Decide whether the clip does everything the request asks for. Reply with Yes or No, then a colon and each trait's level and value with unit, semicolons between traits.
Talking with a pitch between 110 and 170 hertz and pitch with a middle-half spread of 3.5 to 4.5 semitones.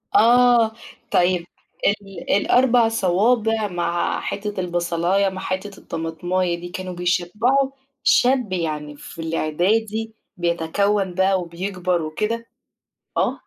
No: medium, 185 Hz; average, 4.0 semitones